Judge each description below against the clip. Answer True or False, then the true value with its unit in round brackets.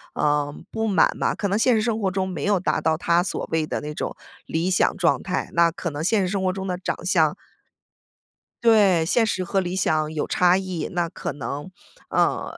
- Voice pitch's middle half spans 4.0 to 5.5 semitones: False (3.1 semitones)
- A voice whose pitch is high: False (180 Hz)